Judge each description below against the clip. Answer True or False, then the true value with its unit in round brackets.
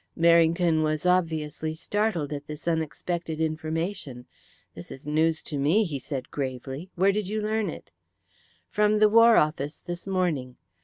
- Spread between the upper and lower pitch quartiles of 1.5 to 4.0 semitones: True (3.7 semitones)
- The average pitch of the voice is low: False (160 Hz)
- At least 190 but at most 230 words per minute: False (150 wpm)